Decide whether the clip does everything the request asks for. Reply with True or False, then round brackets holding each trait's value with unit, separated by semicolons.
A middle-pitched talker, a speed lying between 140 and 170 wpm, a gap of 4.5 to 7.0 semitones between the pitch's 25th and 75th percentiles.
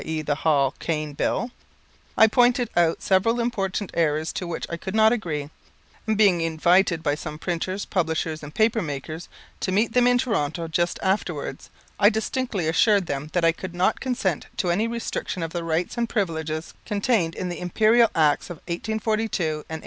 False (175 Hz; 180 wpm; 5.4 semitones)